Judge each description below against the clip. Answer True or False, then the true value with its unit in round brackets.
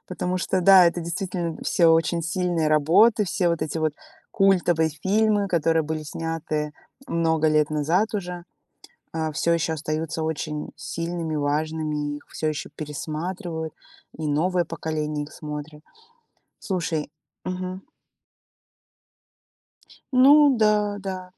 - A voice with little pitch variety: False (3.0 semitones)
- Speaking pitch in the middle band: True (165 Hz)